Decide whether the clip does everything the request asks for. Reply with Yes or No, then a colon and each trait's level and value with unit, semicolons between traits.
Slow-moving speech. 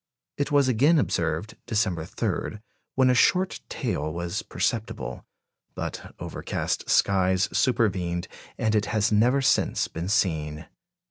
Yes: slow, 125 wpm